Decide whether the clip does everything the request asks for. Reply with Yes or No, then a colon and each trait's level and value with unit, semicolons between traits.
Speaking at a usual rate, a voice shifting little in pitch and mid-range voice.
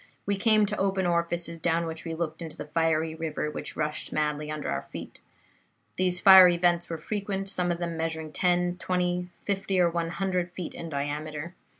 Yes: average, 190 wpm; narrow, 2.2 semitones; medium, 170 Hz